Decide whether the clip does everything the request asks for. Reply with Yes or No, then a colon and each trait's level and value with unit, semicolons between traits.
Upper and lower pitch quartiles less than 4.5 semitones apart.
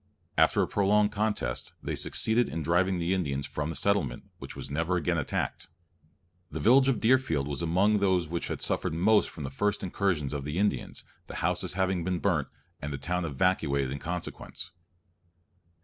No: average, 5.2 semitones